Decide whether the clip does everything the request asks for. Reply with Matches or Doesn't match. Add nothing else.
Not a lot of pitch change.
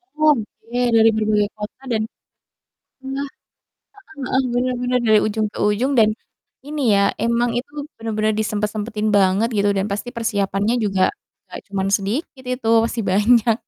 Doesn't match